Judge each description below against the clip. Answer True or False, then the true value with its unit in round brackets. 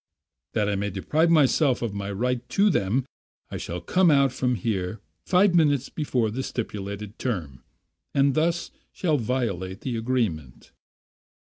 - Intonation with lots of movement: True (5.9 semitones)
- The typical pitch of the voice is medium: False (120 Hz)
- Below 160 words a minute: True (145 wpm)